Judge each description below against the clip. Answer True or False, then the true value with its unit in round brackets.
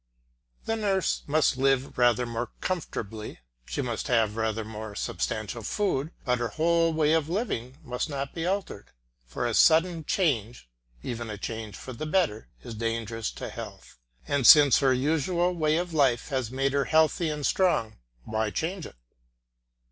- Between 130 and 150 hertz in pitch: True (135 Hz)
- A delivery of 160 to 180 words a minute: True (165 wpm)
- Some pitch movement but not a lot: False (6.0 semitones)